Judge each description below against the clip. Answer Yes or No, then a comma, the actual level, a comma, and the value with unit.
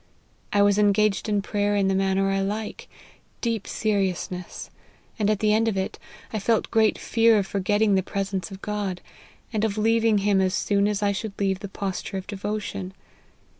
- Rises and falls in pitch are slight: Yes, narrow, 1.6 semitones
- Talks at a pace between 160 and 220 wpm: Yes, average, 180 wpm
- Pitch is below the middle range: No, high, 205 Hz